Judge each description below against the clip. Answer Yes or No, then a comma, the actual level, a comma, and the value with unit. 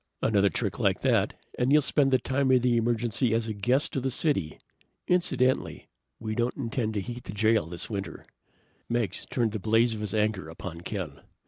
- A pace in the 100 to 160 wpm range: No, average, 195 wpm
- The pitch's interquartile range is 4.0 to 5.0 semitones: No, average, 3.6 semitones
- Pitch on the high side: No, low, 115 Hz